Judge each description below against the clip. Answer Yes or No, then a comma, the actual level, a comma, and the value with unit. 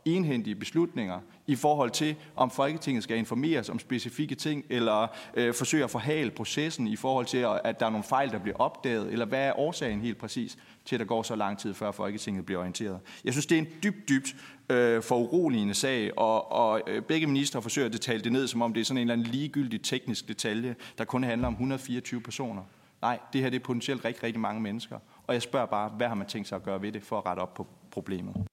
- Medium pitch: No, low, 120 Hz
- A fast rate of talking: Yes, fast, 235 wpm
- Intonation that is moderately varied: Yes, average, 3.5 semitones